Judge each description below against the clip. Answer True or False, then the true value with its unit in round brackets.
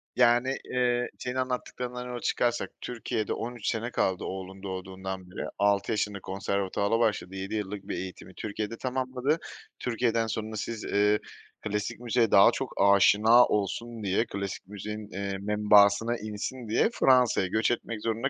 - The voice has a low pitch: True (110 Hz)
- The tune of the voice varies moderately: True (3.3 semitones)